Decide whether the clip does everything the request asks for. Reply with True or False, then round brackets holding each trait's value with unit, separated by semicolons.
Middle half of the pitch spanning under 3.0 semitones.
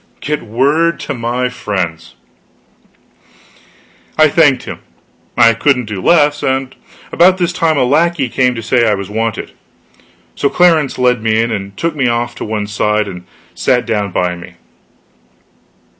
False (5.6 semitones)